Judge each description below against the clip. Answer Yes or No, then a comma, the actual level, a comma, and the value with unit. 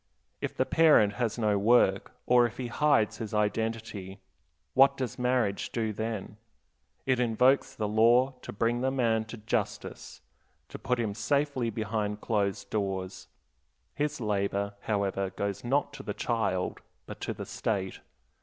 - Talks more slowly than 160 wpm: Yes, average, 150 wpm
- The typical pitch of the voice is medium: No, low, 110 Hz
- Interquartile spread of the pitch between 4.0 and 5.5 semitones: No, average, 3.2 semitones